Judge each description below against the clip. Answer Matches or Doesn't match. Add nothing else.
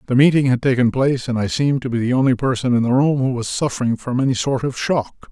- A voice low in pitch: Matches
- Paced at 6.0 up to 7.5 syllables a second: Matches